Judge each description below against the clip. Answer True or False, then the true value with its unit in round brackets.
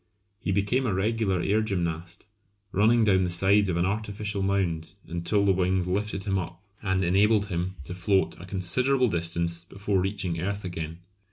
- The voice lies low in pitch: True (95 Hz)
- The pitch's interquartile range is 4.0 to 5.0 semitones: False (2.8 semitones)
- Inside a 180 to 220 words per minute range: False (170 wpm)